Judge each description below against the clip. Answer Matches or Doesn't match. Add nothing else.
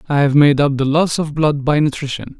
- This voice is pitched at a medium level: Matches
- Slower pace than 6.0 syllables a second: Matches